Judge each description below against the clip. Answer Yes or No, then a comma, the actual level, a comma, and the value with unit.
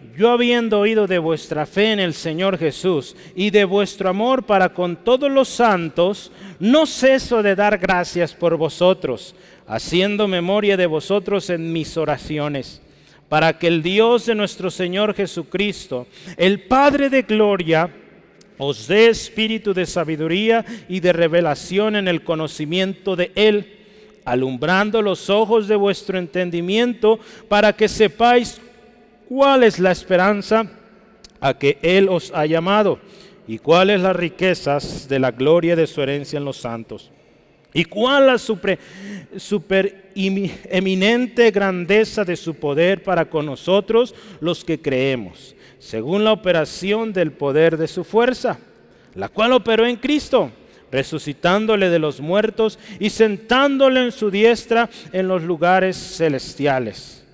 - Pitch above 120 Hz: Yes, high, 190 Hz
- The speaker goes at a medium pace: Yes, average, 140 wpm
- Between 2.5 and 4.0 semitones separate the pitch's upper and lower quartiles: No, average, 4.4 semitones